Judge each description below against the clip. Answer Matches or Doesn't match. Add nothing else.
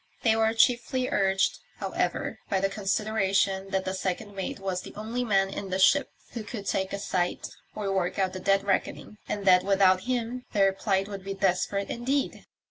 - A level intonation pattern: Matches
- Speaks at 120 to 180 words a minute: Doesn't match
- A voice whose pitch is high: Matches